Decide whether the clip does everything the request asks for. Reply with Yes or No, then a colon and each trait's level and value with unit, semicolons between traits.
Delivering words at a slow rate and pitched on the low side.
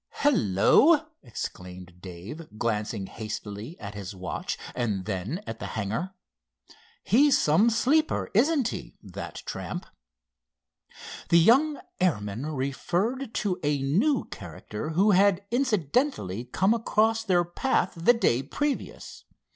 No: slow, 115 wpm; medium, 165 Hz